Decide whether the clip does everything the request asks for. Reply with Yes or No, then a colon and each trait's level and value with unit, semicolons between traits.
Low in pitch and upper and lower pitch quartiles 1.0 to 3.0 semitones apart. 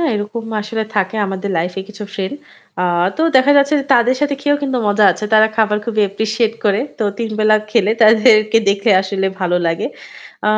No: high, 215 Hz; narrow, 2.5 semitones